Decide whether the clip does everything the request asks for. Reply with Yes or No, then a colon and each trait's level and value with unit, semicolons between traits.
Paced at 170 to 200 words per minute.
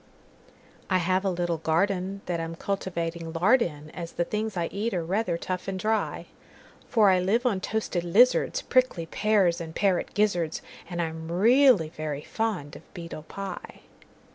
No: average, 140 wpm